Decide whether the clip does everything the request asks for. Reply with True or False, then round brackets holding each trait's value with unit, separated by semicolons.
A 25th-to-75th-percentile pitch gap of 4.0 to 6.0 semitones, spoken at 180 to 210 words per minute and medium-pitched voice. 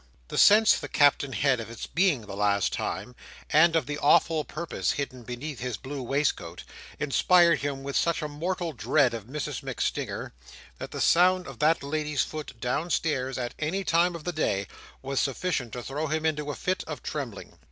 True (4.4 semitones; 185 wpm; 145 Hz)